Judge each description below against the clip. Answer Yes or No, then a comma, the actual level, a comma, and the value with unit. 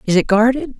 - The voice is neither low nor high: No, high, 225 Hz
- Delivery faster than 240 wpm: No, fast, 225 wpm